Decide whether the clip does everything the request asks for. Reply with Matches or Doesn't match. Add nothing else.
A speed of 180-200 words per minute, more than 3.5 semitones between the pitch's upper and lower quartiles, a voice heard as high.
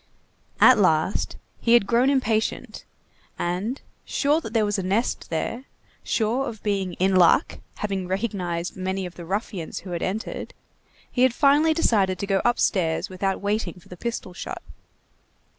Doesn't match